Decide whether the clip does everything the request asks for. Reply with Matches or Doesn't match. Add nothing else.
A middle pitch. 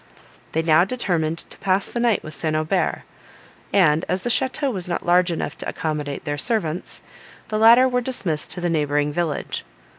Matches